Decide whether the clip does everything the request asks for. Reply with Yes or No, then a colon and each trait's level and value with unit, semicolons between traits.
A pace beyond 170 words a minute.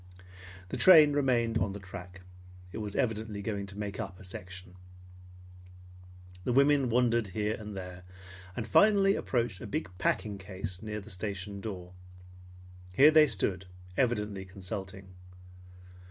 No: average, 140 wpm